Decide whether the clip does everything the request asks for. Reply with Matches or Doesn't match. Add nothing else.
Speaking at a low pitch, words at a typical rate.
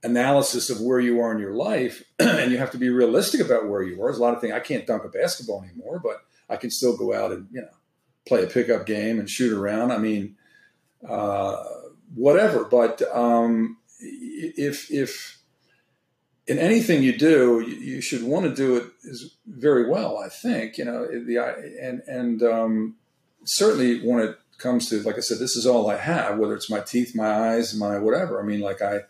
Doesn't match